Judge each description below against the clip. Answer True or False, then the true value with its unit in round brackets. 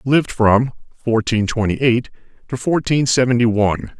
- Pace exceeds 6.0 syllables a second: False (5.0 syllables/s)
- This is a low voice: True (120 Hz)